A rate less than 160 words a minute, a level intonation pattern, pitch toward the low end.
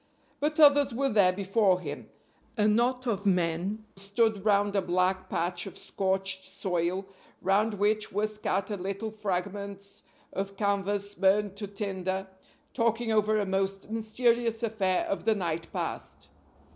No: average, 140 wpm; narrow, 2.3 semitones; high, 200 Hz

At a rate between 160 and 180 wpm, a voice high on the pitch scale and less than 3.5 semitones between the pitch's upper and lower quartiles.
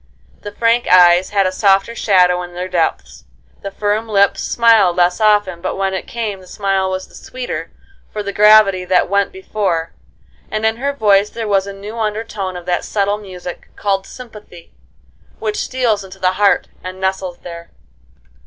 Yes: average, 175 wpm; high, 195 Hz; narrow, 2.6 semitones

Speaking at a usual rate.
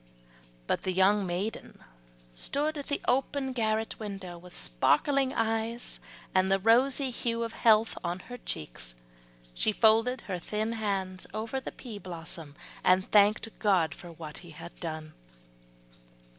Yes: average, 145 wpm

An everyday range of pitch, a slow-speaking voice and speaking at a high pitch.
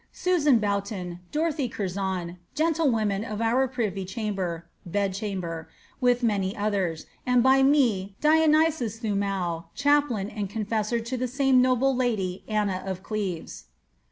Yes: average, 4.9 semitones; slow, 130 wpm; high, 215 Hz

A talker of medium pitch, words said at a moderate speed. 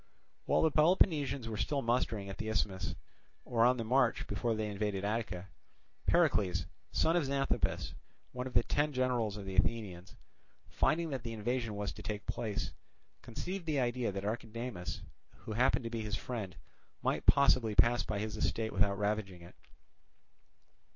No: low, 115 Hz; average, 165 wpm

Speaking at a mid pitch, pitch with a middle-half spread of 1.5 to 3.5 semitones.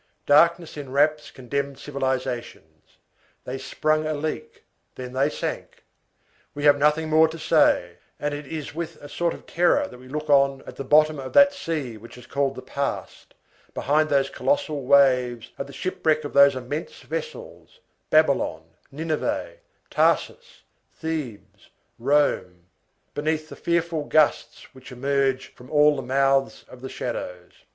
Yes: medium, 145 Hz; average, 2.9 semitones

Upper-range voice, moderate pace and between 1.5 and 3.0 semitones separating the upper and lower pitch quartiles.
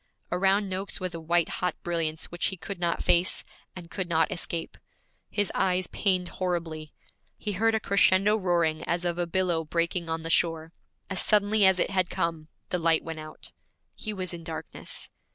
No: medium, 175 Hz; average, 185 wpm; narrow, 2.4 semitones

